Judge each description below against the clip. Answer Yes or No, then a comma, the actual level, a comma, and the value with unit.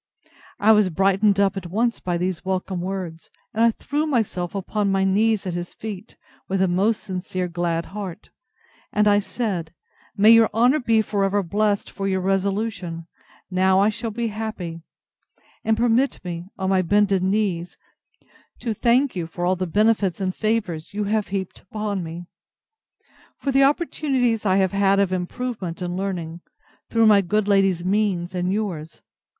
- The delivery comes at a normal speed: Yes, average, 165 wpm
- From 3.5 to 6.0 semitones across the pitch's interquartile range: No, average, 3.0 semitones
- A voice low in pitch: No, high, 195 Hz